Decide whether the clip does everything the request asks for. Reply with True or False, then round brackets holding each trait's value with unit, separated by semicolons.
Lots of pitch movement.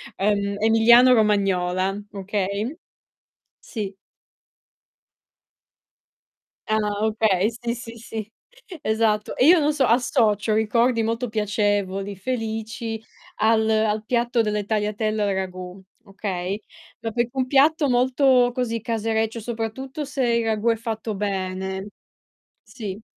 False (2.5 semitones)